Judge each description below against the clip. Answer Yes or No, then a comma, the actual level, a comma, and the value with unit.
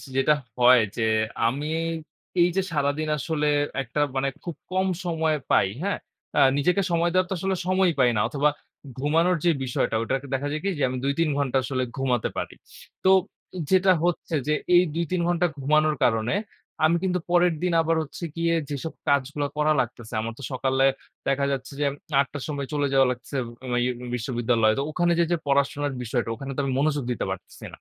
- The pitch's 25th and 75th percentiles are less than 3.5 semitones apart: No, average, 4.3 semitones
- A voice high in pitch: No, medium, 145 Hz